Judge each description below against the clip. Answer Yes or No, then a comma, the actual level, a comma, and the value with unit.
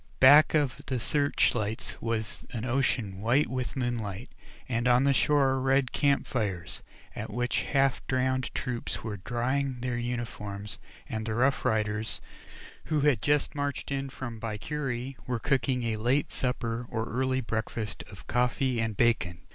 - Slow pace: No, average, 155 wpm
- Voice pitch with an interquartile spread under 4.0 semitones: Yes, average, 3.2 semitones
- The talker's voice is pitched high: No, low, 125 Hz